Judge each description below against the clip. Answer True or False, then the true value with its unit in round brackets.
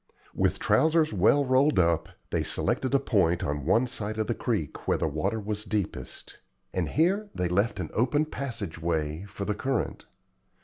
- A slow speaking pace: False (175 wpm)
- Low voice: True (105 Hz)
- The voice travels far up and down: True (7.6 semitones)